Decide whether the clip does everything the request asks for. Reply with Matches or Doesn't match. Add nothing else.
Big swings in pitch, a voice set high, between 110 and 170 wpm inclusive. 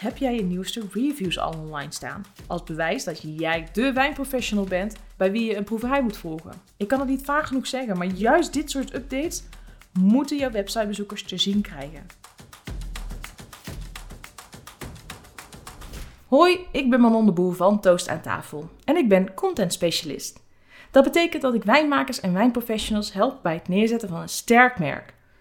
Matches